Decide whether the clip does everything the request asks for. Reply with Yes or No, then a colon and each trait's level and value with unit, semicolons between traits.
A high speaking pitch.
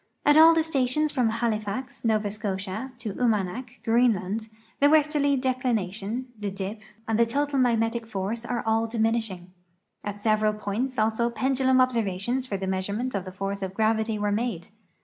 Yes: high, 225 Hz